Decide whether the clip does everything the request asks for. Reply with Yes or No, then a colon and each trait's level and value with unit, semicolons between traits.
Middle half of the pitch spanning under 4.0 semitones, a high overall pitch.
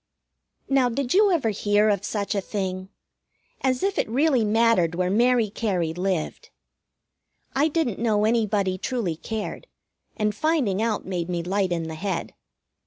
No: average, 4.5 semitones; high, 210 Hz